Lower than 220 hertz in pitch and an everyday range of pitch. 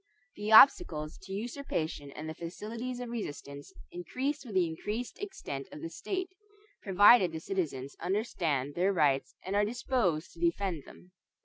No: high, 190 Hz; wide, 6.7 semitones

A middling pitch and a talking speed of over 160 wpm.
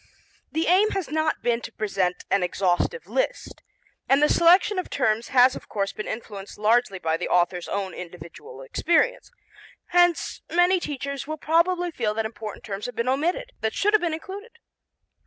No: very high, 255 Hz; average, 175 wpm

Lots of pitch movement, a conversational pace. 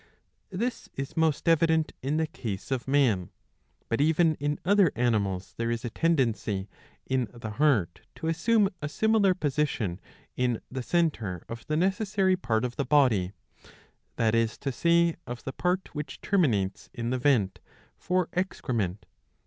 Yes: wide, 6.4 semitones; average, 155 wpm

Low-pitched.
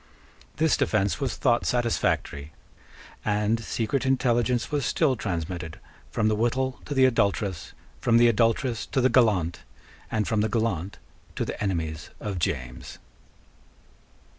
Yes: low, 110 Hz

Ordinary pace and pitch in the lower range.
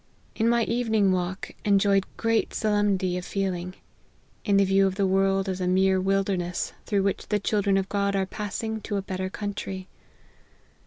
No: average, 170 wpm; high, 195 Hz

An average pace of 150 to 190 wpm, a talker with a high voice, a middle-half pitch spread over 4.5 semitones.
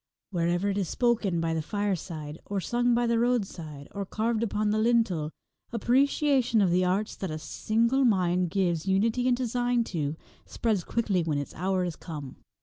Yes: average, 175 wpm; high, 200 Hz; average, 5.3 semitones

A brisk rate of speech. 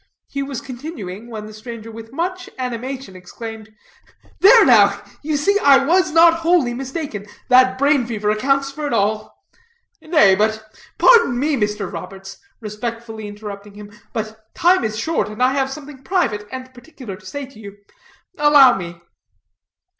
No: average, 160 wpm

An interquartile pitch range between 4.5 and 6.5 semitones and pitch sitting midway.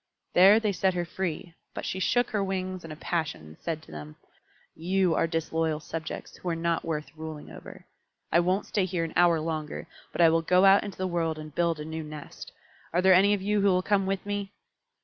No: average, 3.1 semitones; medium, 170 Hz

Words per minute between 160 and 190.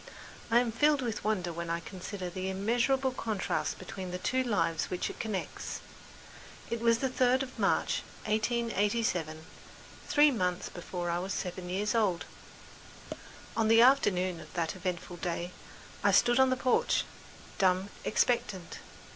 No: average, 145 wpm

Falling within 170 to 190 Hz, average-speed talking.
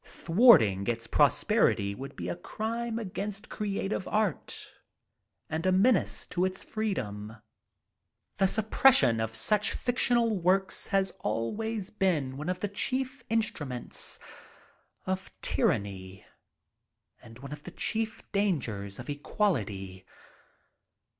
No: medium, 185 Hz; slow, 115 wpm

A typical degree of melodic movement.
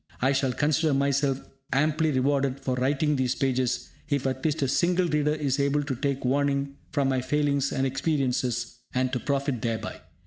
No: narrow, 2.0 semitones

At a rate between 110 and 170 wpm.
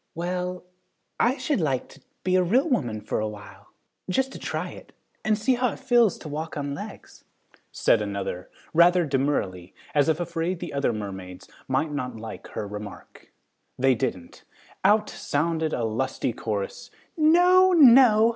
Yes: average, 160 wpm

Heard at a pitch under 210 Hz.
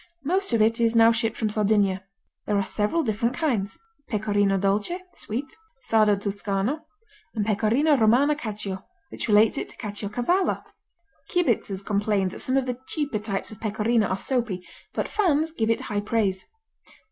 No: high, 220 Hz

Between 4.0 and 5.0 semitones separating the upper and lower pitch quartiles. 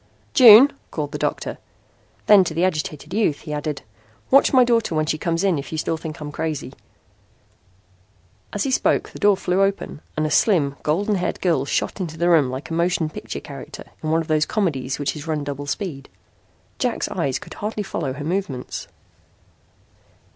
Yes: average, 4.7 semitones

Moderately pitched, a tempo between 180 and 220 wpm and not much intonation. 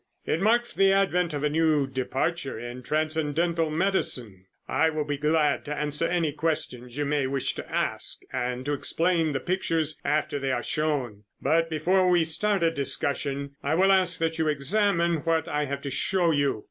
No: medium, 155 Hz; average, 185 wpm; average, 3.2 semitones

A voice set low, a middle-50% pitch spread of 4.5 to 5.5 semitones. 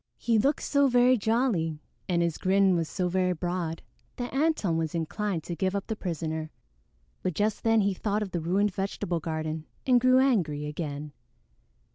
No: medium, 185 Hz; average, 5.2 semitones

